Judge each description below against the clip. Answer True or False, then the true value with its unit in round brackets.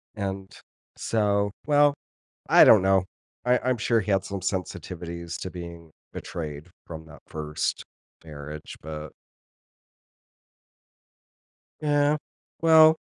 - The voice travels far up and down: True (5.9 semitones)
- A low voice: True (95 Hz)